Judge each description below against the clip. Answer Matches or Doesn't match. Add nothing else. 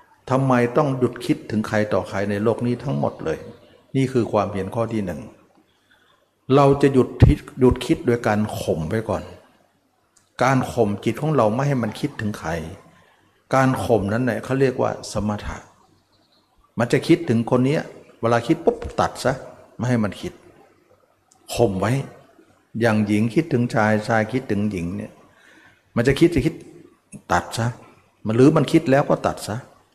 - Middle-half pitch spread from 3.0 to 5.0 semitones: Matches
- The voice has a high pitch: Doesn't match